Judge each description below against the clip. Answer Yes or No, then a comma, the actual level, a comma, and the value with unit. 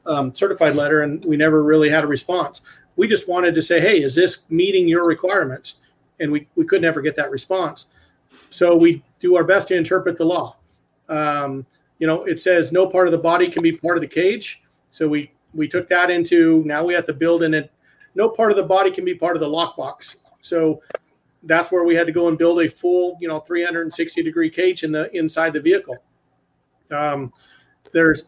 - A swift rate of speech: Yes, fast, 215 wpm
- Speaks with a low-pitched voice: No, medium, 170 Hz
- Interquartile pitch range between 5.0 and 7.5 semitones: No, average, 3.0 semitones